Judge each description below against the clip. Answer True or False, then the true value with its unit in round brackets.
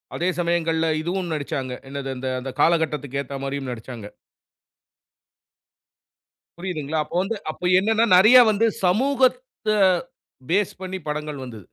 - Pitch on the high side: False (165 Hz)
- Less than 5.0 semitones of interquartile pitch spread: False (5.4 semitones)